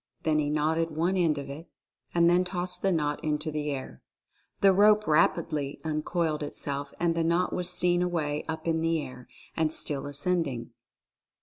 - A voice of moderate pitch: Yes, medium, 160 Hz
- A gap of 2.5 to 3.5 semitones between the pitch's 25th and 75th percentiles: Yes, average, 2.9 semitones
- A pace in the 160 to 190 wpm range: Yes, average, 175 wpm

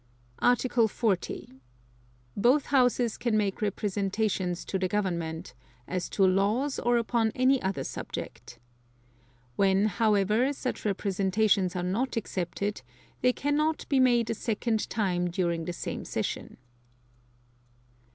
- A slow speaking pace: Yes, slow, 120 wpm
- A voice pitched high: Yes, high, 210 Hz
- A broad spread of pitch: No, average, 4.2 semitones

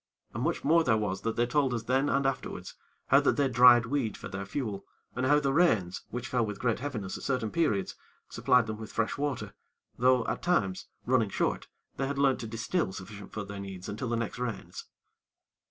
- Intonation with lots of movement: No, average, 4.1 semitones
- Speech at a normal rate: No, fast, 210 wpm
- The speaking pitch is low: Yes, low, 120 Hz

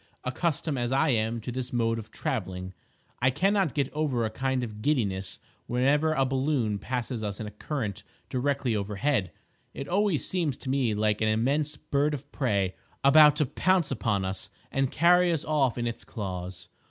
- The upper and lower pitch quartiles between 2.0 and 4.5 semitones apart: No, average, 5.3 semitones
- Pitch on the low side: Yes, low, 130 Hz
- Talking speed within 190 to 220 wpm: No, average, 175 wpm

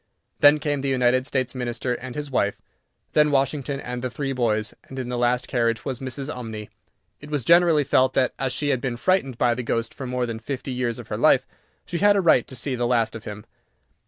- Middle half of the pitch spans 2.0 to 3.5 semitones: Yes, narrow, 2.6 semitones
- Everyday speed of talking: No, fast, 230 wpm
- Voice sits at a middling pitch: No, low, 130 Hz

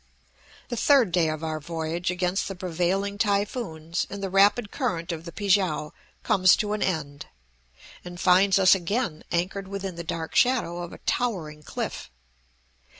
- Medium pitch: Yes, medium, 180 Hz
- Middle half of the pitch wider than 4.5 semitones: No, average, 3.3 semitones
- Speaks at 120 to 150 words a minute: No, average, 160 wpm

